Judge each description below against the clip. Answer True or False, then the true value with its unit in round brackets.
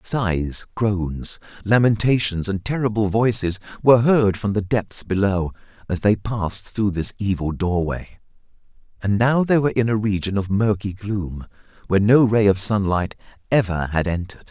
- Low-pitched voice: True (105 Hz)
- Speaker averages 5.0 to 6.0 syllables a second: False (4.7 syllables/s)